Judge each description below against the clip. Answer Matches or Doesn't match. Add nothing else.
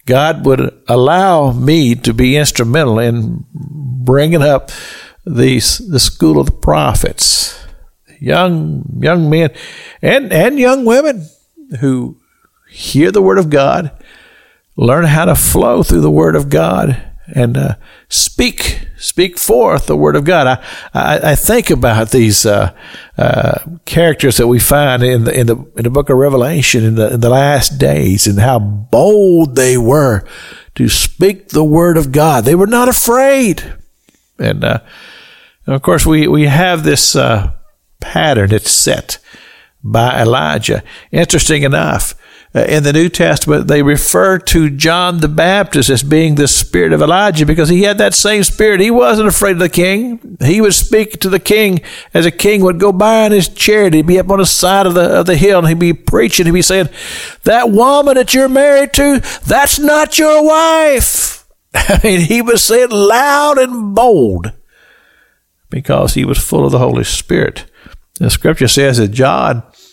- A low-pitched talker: Doesn't match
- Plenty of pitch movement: Matches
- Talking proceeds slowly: Doesn't match